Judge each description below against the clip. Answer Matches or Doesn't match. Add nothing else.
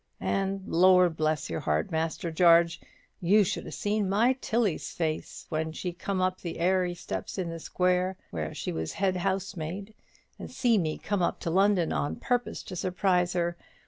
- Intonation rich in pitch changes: Doesn't match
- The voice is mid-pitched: Matches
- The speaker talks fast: Doesn't match